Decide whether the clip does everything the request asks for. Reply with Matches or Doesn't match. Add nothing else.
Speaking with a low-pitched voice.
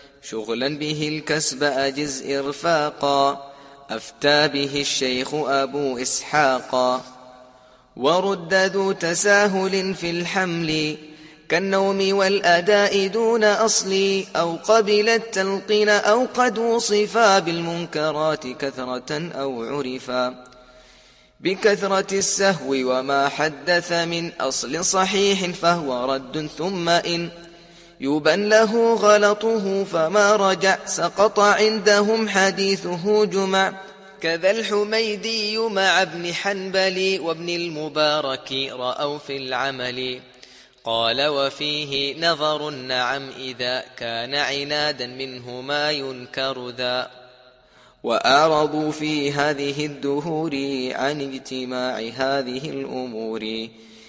Doesn't match